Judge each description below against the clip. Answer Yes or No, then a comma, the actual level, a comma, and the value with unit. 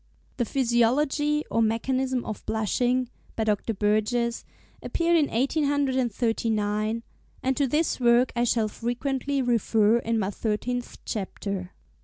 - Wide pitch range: No, average, 3.2 semitones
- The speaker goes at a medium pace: No, slow, 120 wpm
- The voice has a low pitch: No, high, 240 Hz